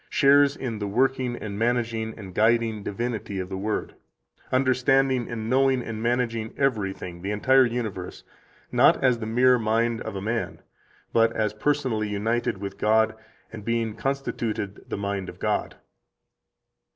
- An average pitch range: Yes, average, 3.0 semitones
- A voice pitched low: Yes, low, 115 Hz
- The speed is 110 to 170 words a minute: Yes, average, 150 wpm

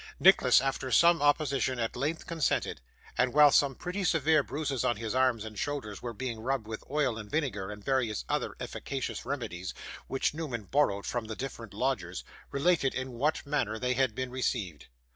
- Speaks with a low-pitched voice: Yes, low, 130 Hz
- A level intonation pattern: No, average, 4.6 semitones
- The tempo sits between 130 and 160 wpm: No, average, 180 wpm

